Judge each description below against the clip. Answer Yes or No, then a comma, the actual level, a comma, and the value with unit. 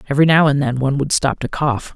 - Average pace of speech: No, fast, 275 wpm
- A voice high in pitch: No, medium, 140 Hz